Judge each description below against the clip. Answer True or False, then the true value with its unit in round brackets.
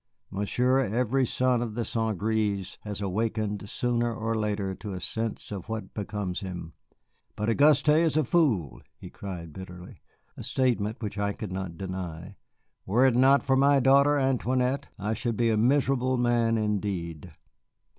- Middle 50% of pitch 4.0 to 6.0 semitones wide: True (4.3 semitones)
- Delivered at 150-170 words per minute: True (160 wpm)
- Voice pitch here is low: True (110 Hz)